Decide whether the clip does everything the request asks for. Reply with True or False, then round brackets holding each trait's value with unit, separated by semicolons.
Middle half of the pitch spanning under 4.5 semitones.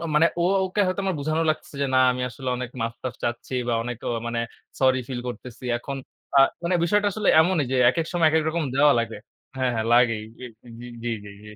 False (5.3 semitones)